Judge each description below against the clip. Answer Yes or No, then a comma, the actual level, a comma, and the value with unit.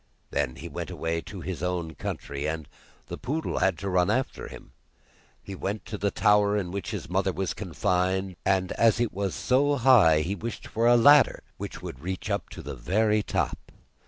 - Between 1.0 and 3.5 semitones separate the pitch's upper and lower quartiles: No, average, 4.0 semitones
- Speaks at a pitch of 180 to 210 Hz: No, very low, 95 Hz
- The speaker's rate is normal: Yes, average, 195 wpm